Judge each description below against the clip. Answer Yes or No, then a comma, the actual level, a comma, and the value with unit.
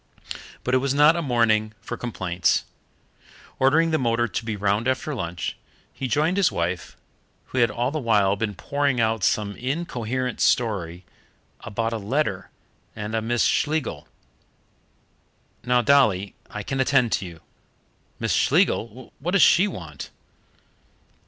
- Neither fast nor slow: Yes, average, 145 wpm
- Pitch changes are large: No, average, 4.7 semitones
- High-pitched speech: No, low, 120 Hz